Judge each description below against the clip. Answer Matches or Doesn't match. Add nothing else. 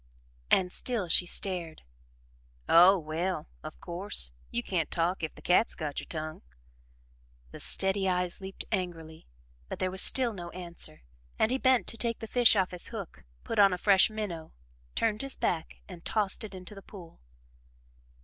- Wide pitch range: Doesn't match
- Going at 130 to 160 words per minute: Doesn't match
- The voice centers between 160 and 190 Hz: Matches